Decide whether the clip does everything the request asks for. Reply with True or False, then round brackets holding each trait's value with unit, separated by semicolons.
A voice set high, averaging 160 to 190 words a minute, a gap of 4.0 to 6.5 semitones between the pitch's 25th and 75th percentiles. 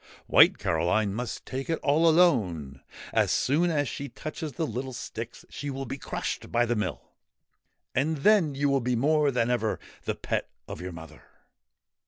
False (135 Hz; 175 wpm; 5.1 semitones)